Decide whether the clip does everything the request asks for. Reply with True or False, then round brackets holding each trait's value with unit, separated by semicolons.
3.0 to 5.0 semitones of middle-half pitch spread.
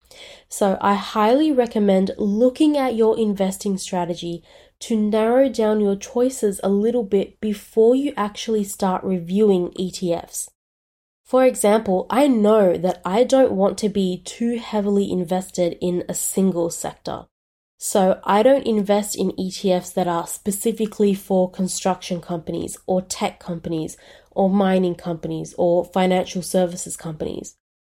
True (3.3 semitones)